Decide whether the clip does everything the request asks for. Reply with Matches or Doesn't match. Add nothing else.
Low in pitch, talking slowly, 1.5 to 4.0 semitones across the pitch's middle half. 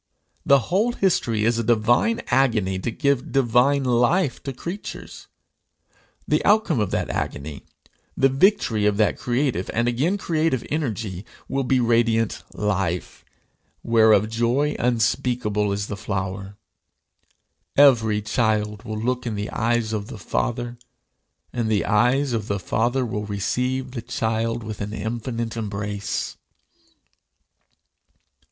Matches